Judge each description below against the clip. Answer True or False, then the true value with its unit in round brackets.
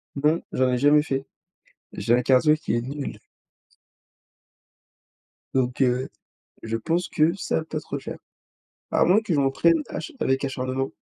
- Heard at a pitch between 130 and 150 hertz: True (135 Hz)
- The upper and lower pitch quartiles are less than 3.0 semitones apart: False (3.3 semitones)